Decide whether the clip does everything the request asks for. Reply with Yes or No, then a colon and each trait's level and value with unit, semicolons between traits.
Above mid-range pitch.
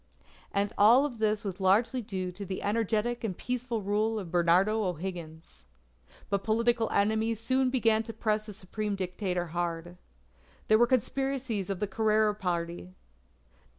Yes: high, 210 Hz